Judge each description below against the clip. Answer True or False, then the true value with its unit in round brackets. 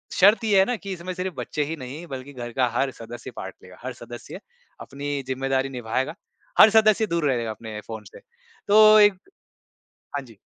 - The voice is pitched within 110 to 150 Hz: True (135 Hz)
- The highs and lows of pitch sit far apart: True (7.4 semitones)